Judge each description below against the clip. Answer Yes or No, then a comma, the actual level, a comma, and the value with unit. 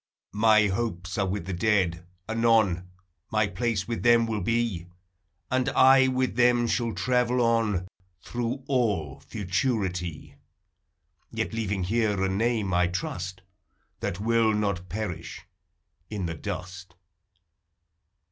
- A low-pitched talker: Yes, low, 105 Hz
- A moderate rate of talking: No, slow, 120 wpm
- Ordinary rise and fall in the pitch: Yes, average, 4.2 semitones